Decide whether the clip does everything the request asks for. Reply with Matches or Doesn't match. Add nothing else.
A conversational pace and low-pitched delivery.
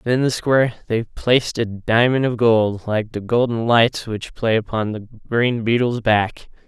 Matches